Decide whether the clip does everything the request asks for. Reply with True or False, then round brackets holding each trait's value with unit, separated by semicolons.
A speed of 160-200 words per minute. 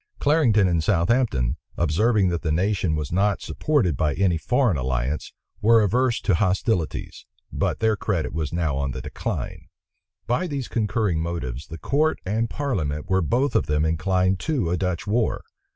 True (165 wpm)